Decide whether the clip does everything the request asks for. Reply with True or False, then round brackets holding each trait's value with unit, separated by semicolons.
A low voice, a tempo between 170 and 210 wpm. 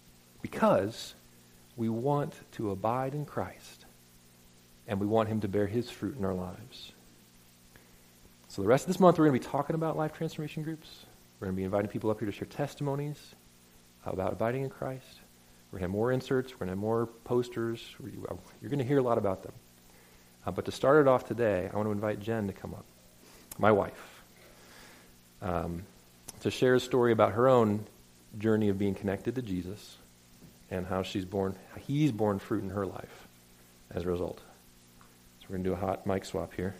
True (95 Hz; 200 wpm)